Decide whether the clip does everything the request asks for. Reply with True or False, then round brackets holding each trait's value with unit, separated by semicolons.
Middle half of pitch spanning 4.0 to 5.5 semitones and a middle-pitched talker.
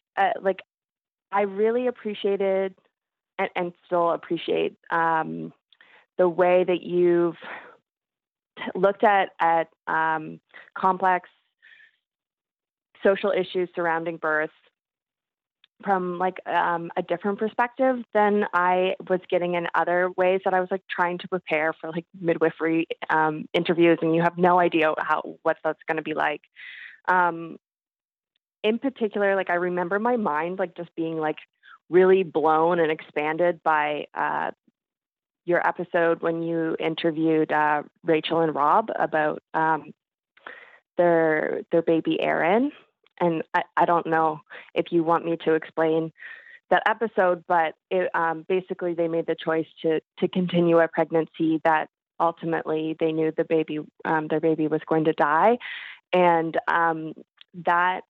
False (2.5 semitones; 170 Hz)